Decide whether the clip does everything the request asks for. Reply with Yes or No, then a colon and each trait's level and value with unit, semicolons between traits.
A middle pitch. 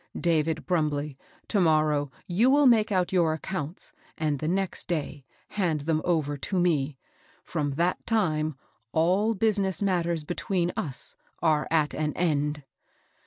Yes: medium, 165 Hz